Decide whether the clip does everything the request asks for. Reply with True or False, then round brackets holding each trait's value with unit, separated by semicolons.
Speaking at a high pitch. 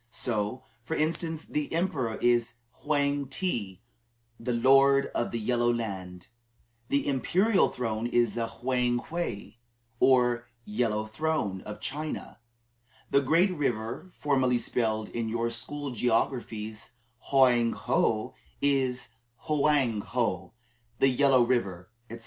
False (120 Hz)